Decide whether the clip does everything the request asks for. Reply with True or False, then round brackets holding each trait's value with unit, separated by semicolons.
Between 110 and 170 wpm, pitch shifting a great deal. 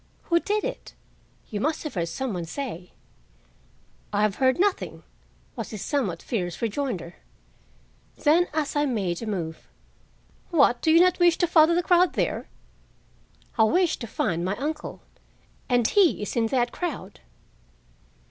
True (155 wpm; 8.3 semitones)